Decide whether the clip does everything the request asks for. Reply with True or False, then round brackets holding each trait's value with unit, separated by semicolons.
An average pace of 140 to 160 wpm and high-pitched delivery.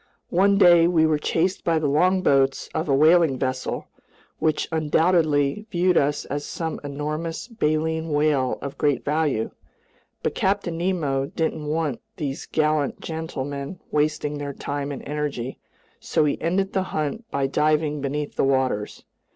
False (145 wpm; 150 Hz)